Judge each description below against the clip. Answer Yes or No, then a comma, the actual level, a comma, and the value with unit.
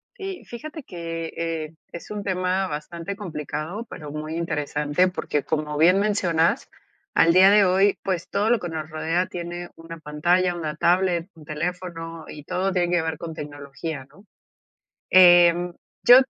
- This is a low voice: No, medium, 170 Hz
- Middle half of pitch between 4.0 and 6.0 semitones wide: No, average, 2.9 semitones